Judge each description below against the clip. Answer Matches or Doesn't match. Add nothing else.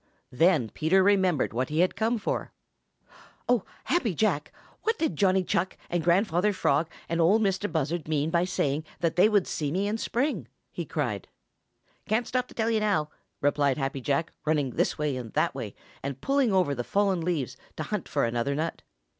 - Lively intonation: Matches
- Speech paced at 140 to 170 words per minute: Doesn't match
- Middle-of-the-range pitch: Matches